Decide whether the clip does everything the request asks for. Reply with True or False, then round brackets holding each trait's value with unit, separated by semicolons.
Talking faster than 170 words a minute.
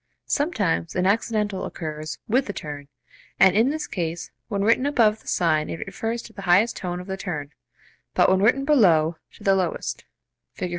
True (185 wpm)